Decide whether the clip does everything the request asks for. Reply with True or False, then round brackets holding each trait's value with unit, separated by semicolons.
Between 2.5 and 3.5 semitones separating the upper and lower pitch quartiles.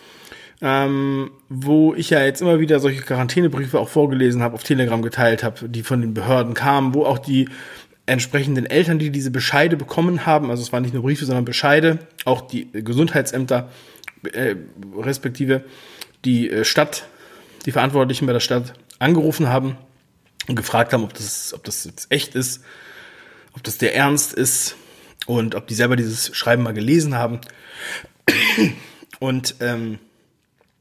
True (2.8 semitones)